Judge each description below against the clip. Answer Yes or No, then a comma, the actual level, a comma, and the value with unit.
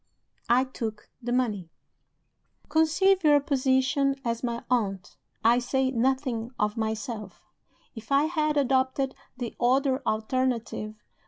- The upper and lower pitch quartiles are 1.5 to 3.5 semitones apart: Yes, average, 3.2 semitones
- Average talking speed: No, slow, 115 wpm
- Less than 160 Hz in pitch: No, very high, 255 Hz